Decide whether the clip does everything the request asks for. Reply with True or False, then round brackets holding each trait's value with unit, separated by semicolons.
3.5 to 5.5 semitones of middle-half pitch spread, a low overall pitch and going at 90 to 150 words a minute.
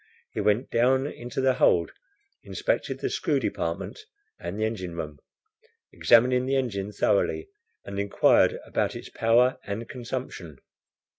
True (4.5 semitones; 115 Hz; 135 wpm)